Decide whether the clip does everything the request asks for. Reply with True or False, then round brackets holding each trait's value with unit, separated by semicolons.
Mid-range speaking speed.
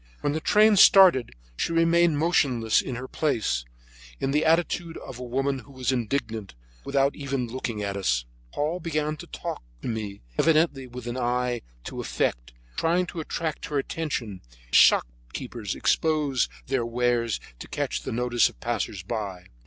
True (160 wpm)